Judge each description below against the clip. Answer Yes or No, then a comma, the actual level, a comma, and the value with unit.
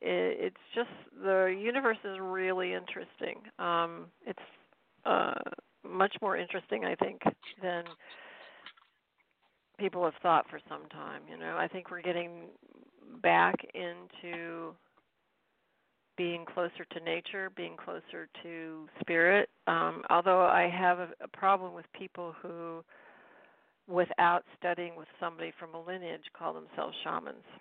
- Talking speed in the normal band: No, slow, 125 wpm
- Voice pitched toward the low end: No, medium, 175 Hz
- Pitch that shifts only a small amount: Yes, narrow, 2.0 semitones